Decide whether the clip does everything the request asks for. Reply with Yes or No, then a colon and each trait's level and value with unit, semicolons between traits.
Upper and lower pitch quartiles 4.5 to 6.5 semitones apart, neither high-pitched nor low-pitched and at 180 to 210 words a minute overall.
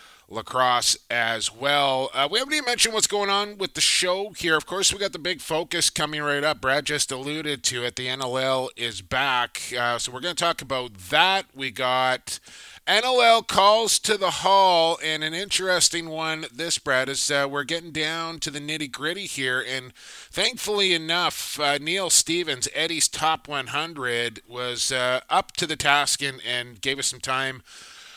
Yes: average, 5.0 semitones; medium, 150 Hz; average, 185 wpm